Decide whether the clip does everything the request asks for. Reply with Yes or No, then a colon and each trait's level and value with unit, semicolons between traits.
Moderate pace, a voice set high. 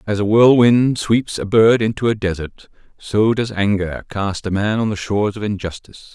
No: average, 195 wpm; low, 105 Hz